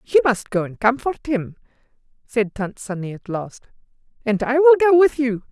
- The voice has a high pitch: Yes, high, 245 Hz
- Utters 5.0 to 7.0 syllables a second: No, 4.8 syllables/s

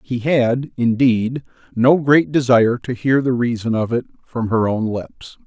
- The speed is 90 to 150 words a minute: No, average, 175 wpm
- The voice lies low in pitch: Yes, low, 120 Hz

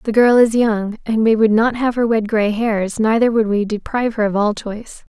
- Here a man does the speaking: No, female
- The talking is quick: Yes, fast, 245 wpm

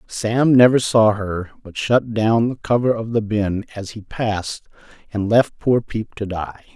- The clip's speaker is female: No, male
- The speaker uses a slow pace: No, average, 185 wpm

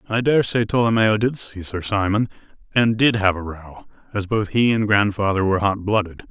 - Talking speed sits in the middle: Yes, average, 190 wpm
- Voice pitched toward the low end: Yes, low, 105 Hz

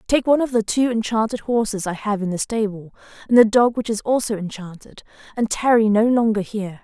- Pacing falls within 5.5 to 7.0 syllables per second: Yes, 5.8 syllables/s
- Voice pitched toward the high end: Yes, high, 220 Hz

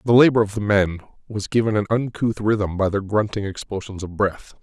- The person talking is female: No, male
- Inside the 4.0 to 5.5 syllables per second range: Yes, 5.4 syllables/s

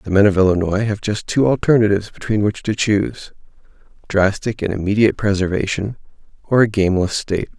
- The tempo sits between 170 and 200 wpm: No, average, 160 wpm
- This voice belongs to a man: Yes, male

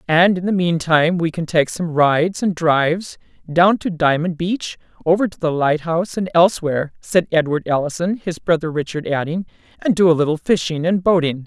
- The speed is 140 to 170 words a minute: No, average, 185 wpm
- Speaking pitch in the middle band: Yes, medium, 170 Hz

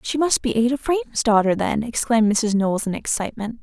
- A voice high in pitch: Yes, high, 230 Hz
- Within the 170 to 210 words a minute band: Yes, average, 200 wpm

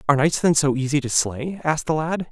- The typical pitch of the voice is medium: Yes, medium, 145 Hz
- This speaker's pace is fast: Yes, fast, 260 wpm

